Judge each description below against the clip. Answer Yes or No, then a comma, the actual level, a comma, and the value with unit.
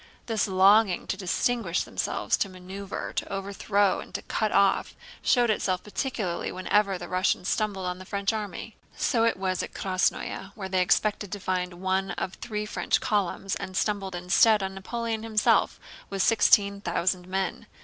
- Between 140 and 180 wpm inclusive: Yes, average, 170 wpm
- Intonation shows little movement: Yes, narrow, 2.1 semitones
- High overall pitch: Yes, high, 195 Hz